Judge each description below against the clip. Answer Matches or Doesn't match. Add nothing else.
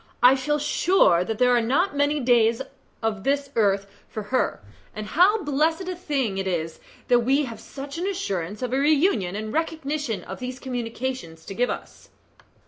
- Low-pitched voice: Doesn't match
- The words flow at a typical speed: Matches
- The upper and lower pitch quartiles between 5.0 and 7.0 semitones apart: Matches